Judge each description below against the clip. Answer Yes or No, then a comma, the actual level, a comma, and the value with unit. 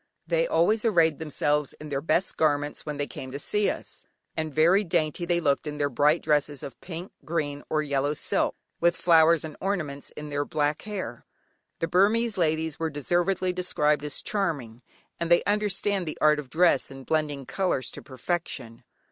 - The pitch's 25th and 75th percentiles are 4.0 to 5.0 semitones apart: No, average, 3.4 semitones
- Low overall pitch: No, medium, 155 Hz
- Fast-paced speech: No, average, 180 wpm